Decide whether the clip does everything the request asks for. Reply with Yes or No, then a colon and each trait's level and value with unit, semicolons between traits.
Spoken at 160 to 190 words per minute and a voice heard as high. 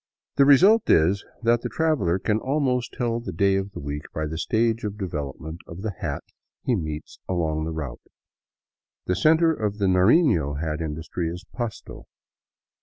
No: average, 170 wpm; very low, 95 Hz